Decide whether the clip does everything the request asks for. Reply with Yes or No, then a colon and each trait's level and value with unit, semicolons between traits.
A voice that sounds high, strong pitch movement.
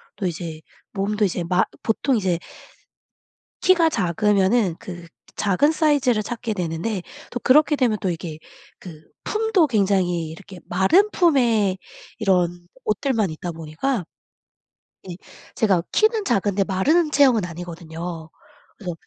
Yes: high, 195 Hz; wide, 6.2 semitones